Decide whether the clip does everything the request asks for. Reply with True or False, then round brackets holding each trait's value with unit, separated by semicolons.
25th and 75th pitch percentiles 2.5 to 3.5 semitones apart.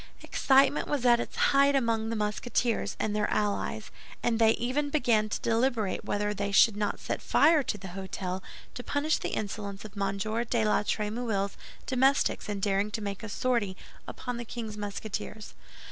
True (3.0 semitones)